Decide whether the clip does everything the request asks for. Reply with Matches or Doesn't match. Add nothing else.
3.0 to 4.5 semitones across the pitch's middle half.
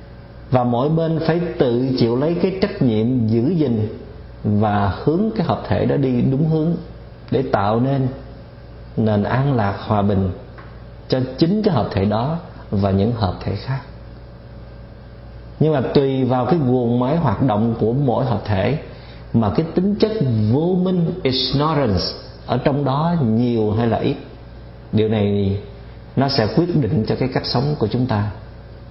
Doesn't match